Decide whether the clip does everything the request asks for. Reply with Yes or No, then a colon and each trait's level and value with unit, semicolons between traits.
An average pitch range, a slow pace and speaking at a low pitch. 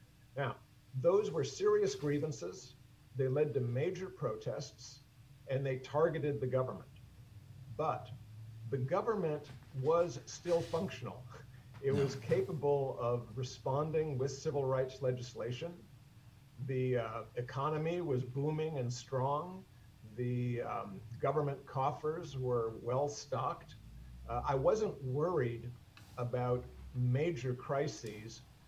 Yes: average, 3.1 semitones; slow, 105 wpm; low, 130 Hz